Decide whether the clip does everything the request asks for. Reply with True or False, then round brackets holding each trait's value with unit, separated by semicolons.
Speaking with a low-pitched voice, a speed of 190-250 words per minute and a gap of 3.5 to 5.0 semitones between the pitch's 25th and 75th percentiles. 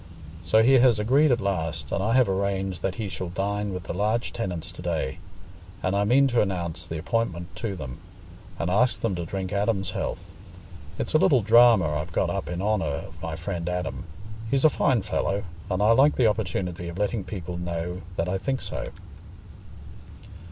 True (95 Hz; 195 wpm; 4.5 semitones)